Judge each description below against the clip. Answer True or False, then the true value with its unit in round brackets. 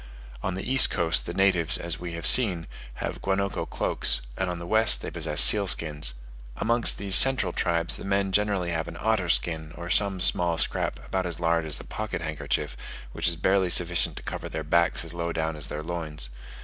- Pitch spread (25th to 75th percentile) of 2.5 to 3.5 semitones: True (2.9 semitones)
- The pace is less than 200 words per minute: False (205 wpm)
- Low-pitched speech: True (85 Hz)